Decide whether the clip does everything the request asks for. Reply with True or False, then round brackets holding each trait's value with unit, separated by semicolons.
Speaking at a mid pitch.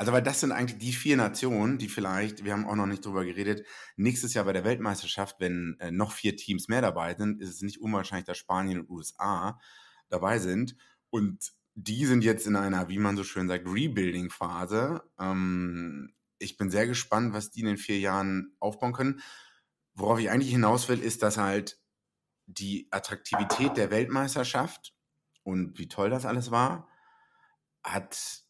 False (105 Hz)